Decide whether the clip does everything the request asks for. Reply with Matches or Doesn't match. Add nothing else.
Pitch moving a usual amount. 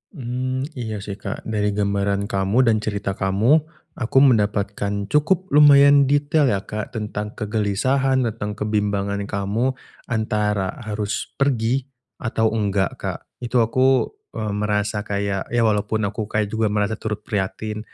Matches